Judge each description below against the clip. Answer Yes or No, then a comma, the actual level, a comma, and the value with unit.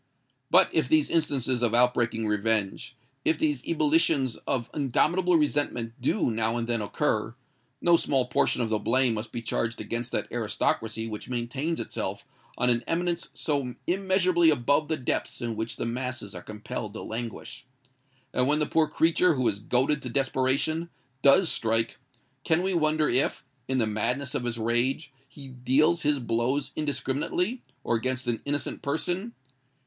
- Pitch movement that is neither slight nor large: Yes, average, 4.7 semitones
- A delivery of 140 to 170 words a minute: Yes, average, 160 wpm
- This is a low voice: Yes, low, 130 Hz